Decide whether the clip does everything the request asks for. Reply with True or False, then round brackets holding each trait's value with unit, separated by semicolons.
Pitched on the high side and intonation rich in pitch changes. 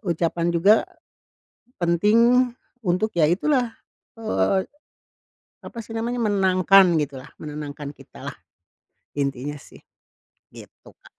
False (180 Hz; 6.5 semitones)